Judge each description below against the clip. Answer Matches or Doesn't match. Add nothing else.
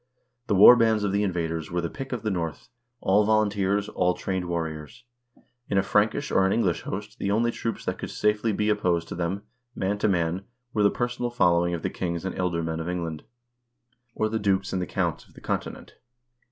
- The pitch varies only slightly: Doesn't match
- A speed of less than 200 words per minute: Doesn't match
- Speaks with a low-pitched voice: Matches